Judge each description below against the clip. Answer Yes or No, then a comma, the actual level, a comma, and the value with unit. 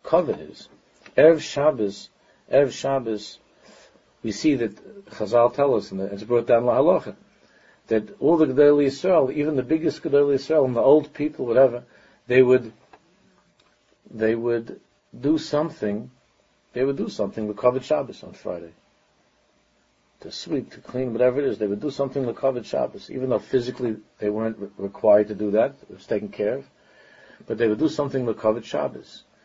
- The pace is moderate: Yes, average, 175 wpm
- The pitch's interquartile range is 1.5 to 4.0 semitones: No, average, 4.7 semitones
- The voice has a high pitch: No, low, 125 Hz